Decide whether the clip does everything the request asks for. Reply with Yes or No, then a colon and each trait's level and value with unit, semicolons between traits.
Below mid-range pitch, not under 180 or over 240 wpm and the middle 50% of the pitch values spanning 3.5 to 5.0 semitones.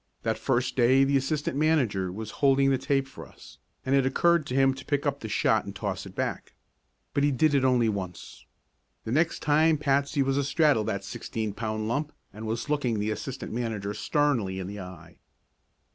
Yes: low, 130 Hz; average, 200 wpm; average, 4.6 semitones